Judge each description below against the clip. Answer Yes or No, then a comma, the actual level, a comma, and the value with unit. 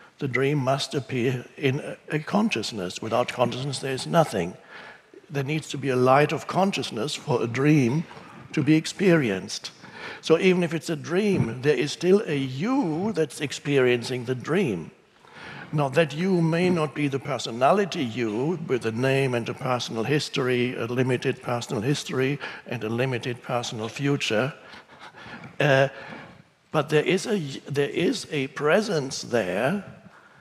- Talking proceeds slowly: No, average, 150 wpm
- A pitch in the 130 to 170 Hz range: Yes, medium, 140 Hz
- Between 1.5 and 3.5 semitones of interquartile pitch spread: No, average, 3.9 semitones